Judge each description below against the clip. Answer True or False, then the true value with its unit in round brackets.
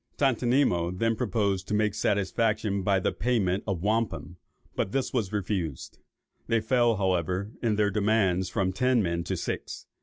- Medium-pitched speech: False (105 Hz)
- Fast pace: False (155 wpm)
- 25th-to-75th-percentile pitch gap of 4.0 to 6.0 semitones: False (3.4 semitones)